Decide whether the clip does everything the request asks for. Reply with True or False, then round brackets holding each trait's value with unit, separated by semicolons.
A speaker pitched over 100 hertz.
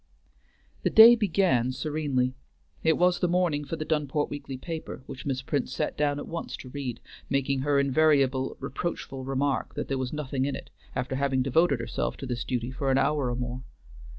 True (140 Hz)